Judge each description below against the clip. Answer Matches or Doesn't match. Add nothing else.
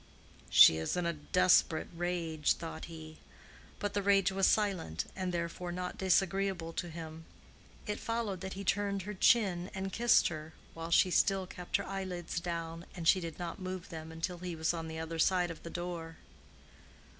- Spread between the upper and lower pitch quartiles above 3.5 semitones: Doesn't match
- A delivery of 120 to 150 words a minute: Doesn't match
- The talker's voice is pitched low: Doesn't match